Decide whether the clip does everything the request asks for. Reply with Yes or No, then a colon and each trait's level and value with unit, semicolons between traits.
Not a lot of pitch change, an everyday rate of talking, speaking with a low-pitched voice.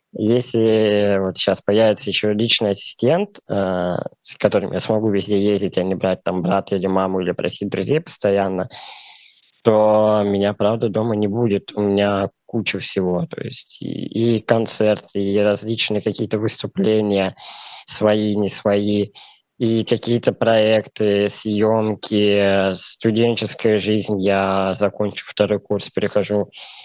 Yes: narrow, 1.7 semitones; average, 130 wpm; low, 105 Hz